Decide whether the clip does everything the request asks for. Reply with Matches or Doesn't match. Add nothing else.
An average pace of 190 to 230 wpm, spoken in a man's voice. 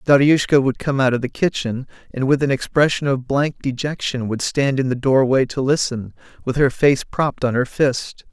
Matches